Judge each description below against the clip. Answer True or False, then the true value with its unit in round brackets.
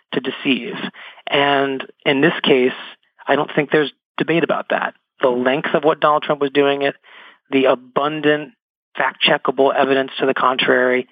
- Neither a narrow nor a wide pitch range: False (2.0 semitones)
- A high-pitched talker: False (140 Hz)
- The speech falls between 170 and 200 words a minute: False (160 wpm)